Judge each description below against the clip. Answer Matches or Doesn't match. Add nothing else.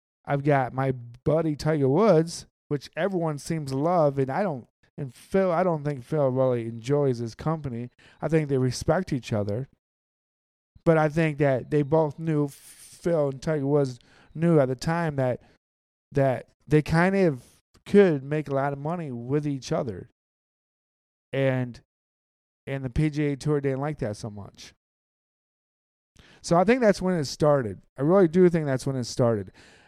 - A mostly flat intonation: Doesn't match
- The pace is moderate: Matches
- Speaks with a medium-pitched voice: Matches